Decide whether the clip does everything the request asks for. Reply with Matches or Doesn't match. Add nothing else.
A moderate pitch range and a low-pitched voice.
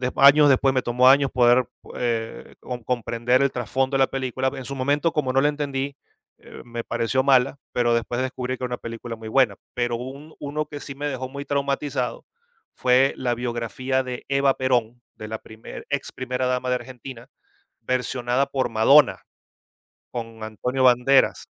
Doesn't match